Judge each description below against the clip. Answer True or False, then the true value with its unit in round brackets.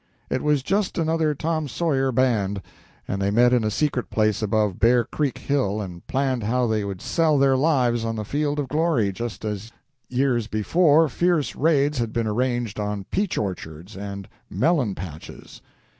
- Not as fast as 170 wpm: False (175 wpm)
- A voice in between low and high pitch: False (120 Hz)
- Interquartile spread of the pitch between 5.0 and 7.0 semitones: True (5.6 semitones)